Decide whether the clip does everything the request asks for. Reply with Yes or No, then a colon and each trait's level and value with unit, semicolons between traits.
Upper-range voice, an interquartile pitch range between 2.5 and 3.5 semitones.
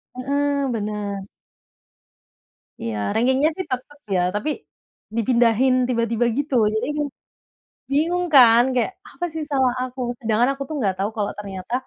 No: high, 245 Hz; average, 4.5 semitones